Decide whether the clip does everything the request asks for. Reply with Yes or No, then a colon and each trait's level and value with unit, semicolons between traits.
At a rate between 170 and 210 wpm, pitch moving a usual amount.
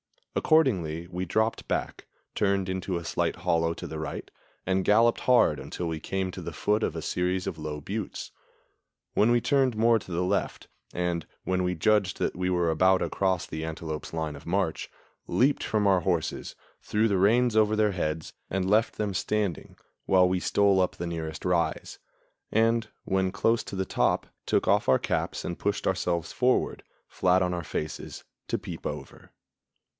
Yes: average, 180 wpm; average, 3.8 semitones